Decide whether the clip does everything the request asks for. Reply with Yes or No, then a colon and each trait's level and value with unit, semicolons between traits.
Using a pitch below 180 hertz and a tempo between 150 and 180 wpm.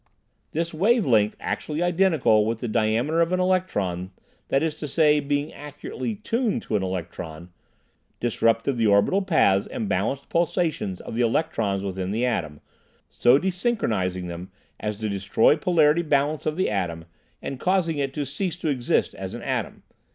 Yes: medium, 140 Hz; average, 165 wpm